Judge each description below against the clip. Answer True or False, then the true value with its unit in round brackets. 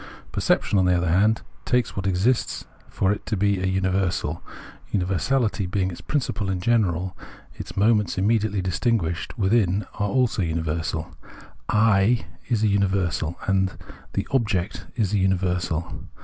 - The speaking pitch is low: True (95 Hz)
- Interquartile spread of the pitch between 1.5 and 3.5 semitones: True (3.0 semitones)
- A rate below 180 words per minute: True (145 wpm)